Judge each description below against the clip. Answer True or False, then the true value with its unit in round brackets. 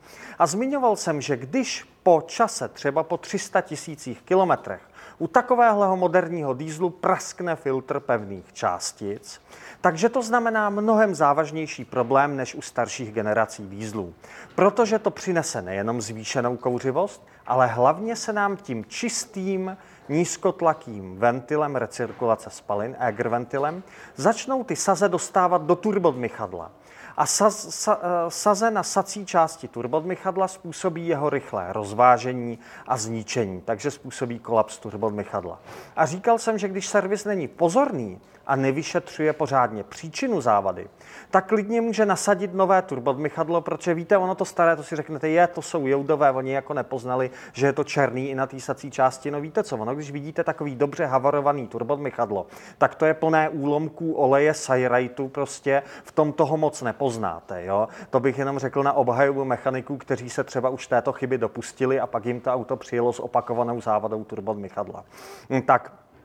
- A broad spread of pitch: True (6.6 semitones)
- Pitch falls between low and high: True (145 Hz)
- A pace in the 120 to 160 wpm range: True (150 wpm)